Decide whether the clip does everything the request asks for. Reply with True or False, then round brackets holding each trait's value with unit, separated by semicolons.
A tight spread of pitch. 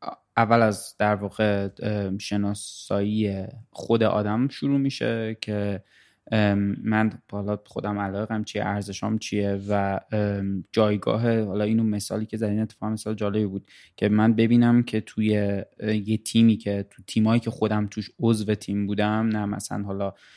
True (1.4 semitones)